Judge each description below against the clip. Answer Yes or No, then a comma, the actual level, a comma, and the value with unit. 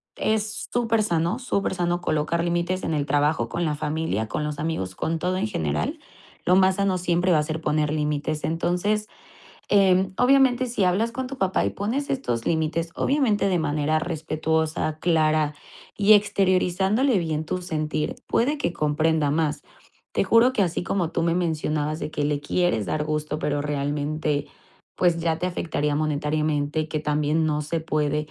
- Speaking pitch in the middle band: Yes, medium, 160 Hz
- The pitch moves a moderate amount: Yes, average, 3.8 semitones